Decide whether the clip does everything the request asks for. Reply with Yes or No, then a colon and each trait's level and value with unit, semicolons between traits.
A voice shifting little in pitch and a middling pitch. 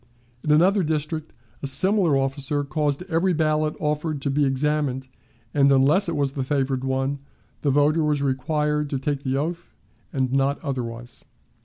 Yes: narrow, 2.2 semitones; medium, 145 Hz